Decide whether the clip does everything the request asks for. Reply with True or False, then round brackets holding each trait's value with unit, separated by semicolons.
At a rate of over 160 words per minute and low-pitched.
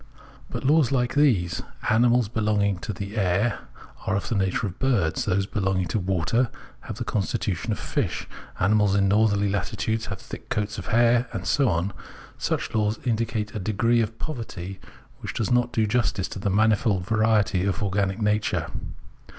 True (175 wpm; 105 Hz)